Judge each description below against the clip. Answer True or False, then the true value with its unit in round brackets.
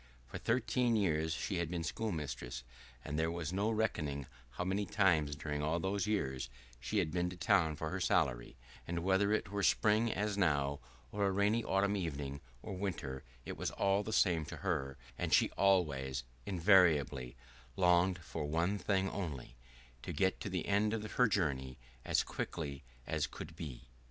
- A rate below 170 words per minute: False (175 wpm)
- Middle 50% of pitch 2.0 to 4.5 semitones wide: False (5.2 semitones)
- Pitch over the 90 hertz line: False (85 Hz)